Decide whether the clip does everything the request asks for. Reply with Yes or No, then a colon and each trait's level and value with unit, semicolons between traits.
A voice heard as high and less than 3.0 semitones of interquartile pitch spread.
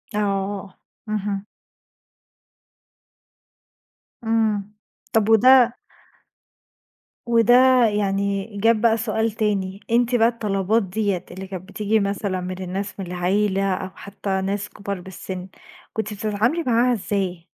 Yes: high, 205 Hz; narrow, 2.5 semitones